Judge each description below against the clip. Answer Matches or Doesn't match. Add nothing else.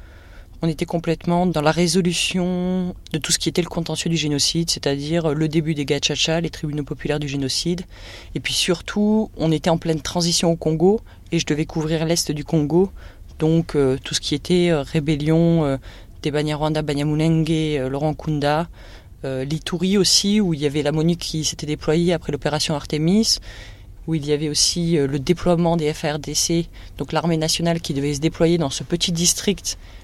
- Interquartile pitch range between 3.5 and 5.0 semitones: Doesn't match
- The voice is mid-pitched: Matches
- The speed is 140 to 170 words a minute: Doesn't match